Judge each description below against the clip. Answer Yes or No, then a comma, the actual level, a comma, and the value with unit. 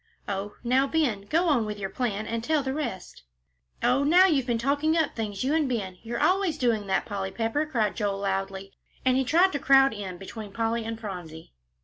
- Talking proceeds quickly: Yes, fast, 210 wpm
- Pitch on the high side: Yes, high, 230 Hz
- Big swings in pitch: Yes, wide, 5.7 semitones